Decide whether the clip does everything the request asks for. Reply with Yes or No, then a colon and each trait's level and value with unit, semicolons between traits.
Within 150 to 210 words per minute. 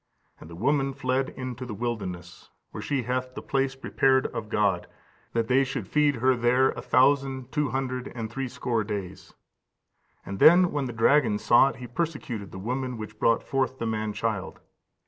Yes: average, 180 wpm